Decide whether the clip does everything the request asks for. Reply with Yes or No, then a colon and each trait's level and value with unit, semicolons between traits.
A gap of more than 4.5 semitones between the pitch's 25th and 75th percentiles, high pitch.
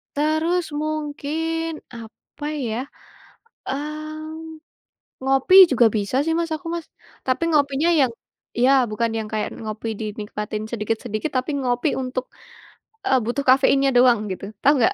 Yes: average, 5.2 semitones; very high, 270 Hz